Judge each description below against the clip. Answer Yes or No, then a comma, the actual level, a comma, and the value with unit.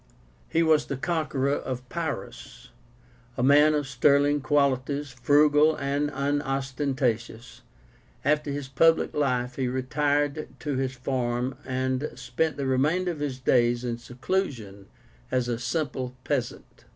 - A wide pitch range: No, narrow, 2.6 semitones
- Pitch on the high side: No, low, 135 Hz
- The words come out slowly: Yes, slow, 125 wpm